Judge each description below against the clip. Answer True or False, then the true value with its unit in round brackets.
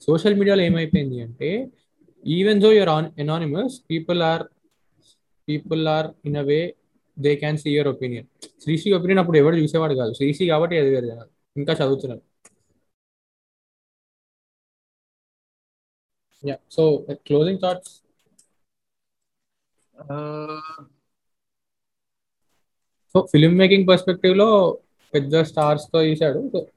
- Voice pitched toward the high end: False (155 Hz)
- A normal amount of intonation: True (3.8 semitones)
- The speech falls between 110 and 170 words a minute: False (95 wpm)